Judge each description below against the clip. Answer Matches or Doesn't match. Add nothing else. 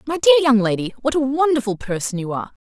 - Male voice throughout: Doesn't match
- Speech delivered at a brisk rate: Matches